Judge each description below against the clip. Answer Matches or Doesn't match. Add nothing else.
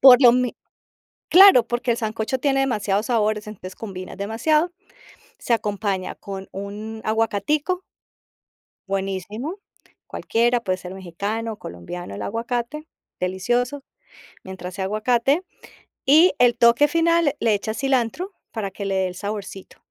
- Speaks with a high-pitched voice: Matches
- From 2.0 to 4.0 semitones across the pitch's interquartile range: Doesn't match